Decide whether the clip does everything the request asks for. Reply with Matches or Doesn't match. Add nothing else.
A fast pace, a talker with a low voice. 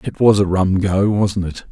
Matches